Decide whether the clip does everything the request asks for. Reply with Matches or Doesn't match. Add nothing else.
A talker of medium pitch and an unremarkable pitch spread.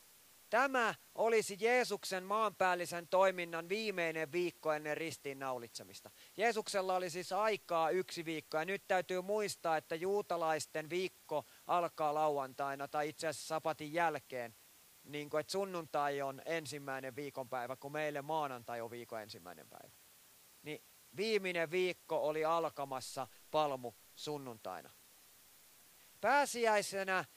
Matches